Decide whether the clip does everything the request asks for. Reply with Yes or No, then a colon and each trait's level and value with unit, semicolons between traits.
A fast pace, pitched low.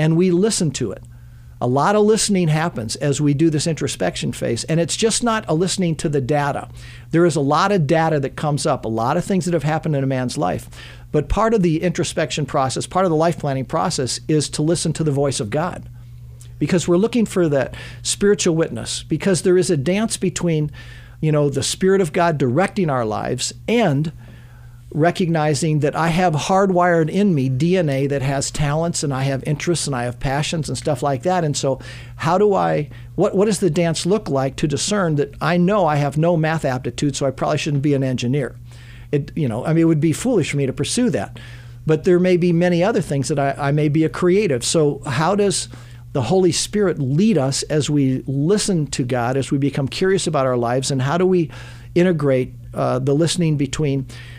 No: fast, 215 wpm; medium, 150 Hz